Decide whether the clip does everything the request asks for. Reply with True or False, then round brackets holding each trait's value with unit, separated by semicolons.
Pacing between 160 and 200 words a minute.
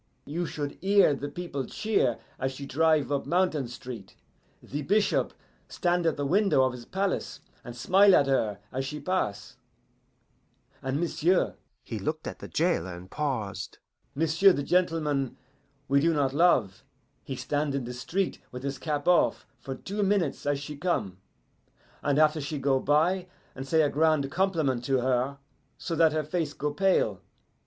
True (165 wpm)